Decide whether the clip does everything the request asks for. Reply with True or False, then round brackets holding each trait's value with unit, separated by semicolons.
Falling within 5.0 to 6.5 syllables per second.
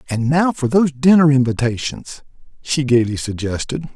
True (5.1 syllables/s)